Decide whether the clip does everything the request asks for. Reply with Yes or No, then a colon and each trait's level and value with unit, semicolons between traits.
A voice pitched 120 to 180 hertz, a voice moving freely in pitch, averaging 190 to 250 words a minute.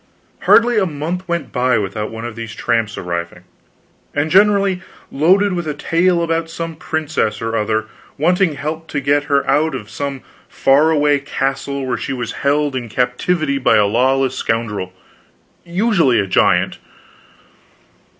No: medium, 140 Hz; wide, 5.7 semitones; average, 150 wpm